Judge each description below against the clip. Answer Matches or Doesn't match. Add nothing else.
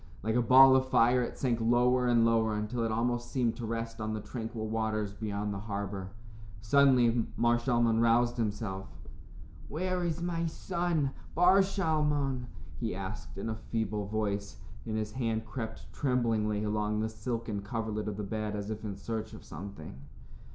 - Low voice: Matches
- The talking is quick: Doesn't match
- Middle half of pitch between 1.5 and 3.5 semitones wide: Matches